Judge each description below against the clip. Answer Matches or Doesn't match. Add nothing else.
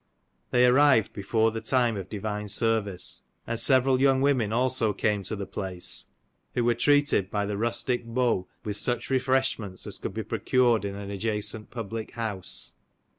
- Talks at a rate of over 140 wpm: Matches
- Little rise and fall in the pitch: Doesn't match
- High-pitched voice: Doesn't match